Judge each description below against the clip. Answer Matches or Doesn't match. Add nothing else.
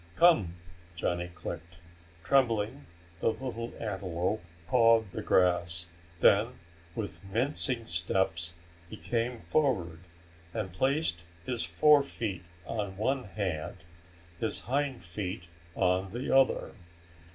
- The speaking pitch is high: Doesn't match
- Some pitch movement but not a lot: Doesn't match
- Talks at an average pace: Doesn't match